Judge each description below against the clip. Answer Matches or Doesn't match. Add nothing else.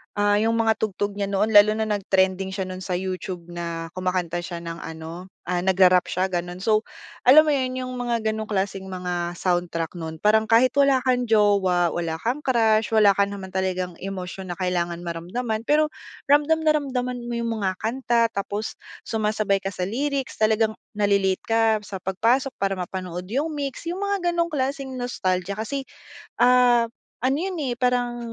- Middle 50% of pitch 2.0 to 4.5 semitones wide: Doesn't match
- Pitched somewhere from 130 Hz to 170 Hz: Doesn't match